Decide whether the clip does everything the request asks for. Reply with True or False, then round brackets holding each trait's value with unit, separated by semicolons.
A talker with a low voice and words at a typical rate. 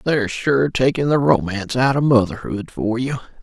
True (125 Hz; 160 wpm)